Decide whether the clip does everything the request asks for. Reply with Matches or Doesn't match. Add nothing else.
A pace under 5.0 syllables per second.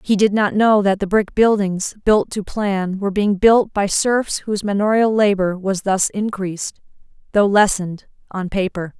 Matches